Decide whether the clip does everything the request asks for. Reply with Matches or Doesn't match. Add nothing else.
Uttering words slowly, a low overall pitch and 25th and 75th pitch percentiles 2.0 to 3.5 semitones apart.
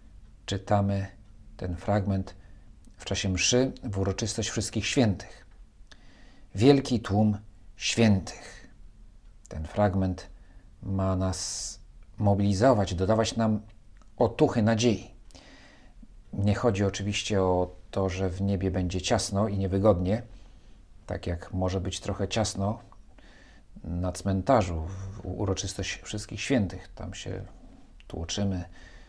Matches